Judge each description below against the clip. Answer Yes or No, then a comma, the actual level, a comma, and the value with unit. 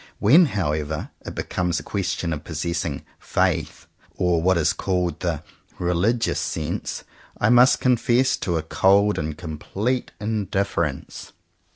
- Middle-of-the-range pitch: No, very low, 90 Hz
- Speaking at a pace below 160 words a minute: Yes, slow, 135 wpm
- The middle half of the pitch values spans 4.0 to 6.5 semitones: Yes, average, 4.3 semitones